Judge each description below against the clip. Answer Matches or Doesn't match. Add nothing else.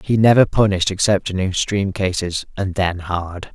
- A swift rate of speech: Doesn't match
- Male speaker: Matches